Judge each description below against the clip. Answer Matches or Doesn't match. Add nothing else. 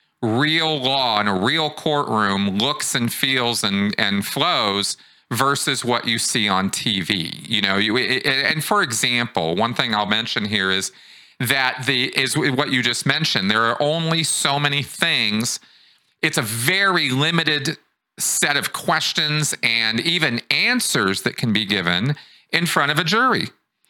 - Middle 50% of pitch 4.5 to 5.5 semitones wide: Matches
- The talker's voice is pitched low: Matches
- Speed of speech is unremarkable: Matches